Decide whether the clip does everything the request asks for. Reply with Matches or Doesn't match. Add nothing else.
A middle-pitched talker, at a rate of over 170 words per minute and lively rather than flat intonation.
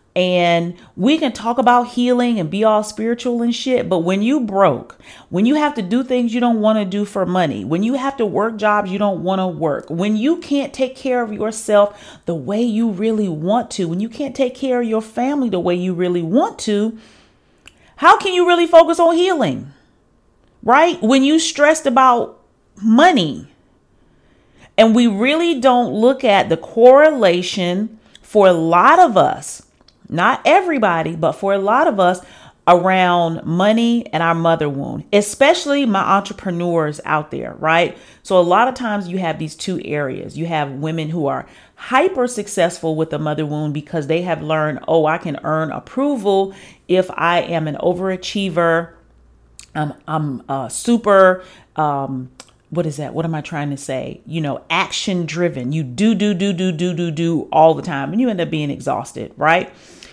Doesn't match